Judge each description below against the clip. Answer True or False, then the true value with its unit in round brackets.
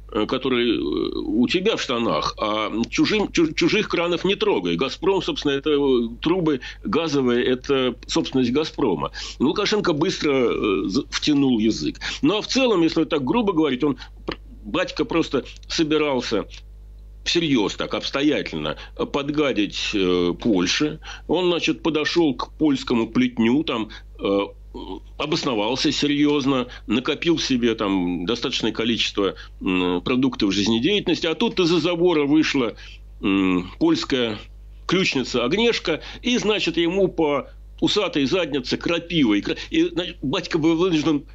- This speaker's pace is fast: False (115 wpm)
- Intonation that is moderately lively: False (8.1 semitones)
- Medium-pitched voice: True (160 Hz)